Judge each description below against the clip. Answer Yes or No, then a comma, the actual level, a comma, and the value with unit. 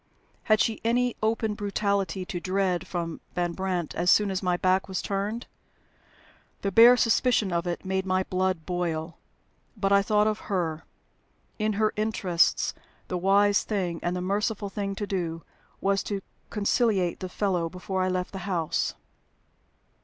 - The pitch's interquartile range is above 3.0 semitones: No, narrow, 2.6 semitones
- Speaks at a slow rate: No, average, 160 wpm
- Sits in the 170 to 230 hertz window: Yes, high, 190 Hz